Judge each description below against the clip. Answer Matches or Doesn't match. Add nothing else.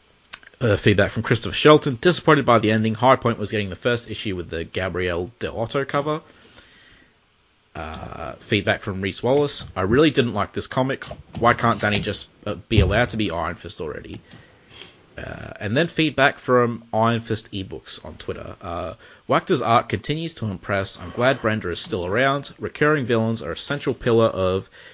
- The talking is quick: Doesn't match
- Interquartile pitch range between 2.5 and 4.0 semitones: Doesn't match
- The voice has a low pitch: Matches